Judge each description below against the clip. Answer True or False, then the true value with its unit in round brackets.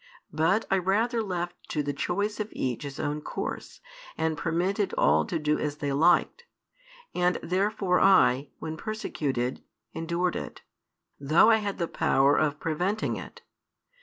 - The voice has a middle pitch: True (170 Hz)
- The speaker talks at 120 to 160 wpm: True (150 wpm)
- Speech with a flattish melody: False (4.8 semitones)